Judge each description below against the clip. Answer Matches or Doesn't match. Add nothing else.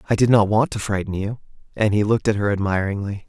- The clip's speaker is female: Doesn't match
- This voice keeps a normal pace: Doesn't match